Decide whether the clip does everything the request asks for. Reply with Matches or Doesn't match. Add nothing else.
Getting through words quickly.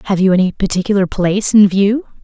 Doesn't match